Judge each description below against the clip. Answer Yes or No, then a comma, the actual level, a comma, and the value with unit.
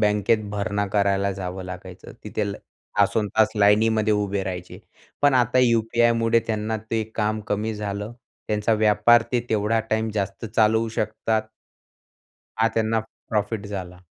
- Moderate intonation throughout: No, narrow, 1.7 semitones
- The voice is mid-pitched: No, low, 105 Hz